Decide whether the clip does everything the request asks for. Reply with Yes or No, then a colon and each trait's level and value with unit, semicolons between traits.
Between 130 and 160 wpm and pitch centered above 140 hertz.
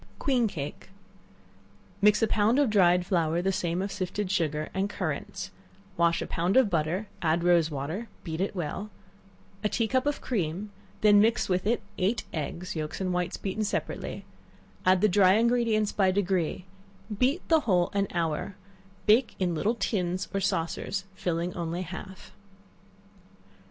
Yes: average, 155 wpm; high, 190 Hz